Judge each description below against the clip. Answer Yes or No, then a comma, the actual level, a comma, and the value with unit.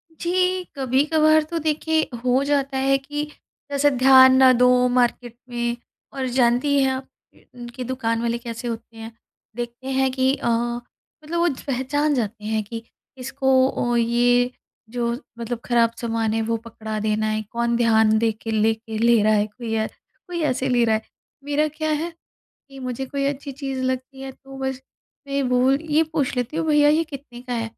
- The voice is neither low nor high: No, very high, 255 Hz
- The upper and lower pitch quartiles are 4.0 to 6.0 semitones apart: No, average, 3.0 semitones